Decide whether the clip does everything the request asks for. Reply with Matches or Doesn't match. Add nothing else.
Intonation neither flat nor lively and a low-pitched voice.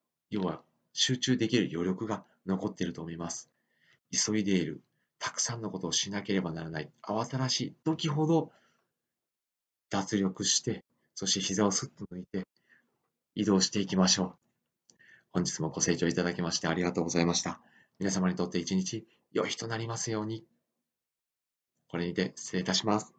Matches